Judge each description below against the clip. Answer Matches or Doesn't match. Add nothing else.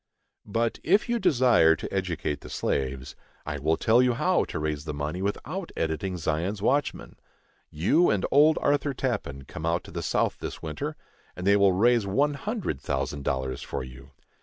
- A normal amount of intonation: Doesn't match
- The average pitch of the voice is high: Doesn't match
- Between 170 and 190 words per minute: Matches